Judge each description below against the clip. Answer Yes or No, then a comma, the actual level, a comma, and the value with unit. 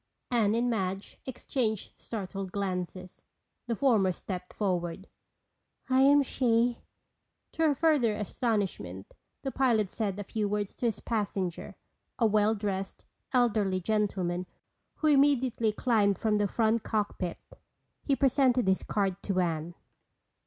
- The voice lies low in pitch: No, high, 210 Hz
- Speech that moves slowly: Yes, slow, 130 wpm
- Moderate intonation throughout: Yes, average, 4.0 semitones